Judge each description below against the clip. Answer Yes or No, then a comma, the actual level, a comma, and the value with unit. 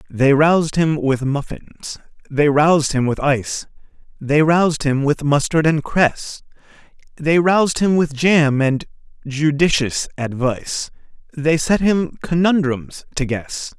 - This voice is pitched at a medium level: Yes, medium, 150 Hz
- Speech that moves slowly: Yes, slow, 130 wpm